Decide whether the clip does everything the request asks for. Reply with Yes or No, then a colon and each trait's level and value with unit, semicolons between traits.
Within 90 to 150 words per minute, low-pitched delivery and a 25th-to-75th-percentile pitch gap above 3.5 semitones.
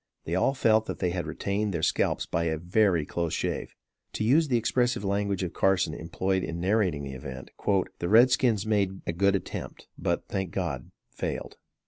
No: average, 185 wpm; very low, 95 Hz; average, 4.1 semitones